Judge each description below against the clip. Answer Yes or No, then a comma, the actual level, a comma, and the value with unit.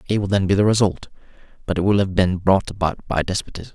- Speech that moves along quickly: Yes, fast, 240 wpm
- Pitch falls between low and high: No, very low, 95 Hz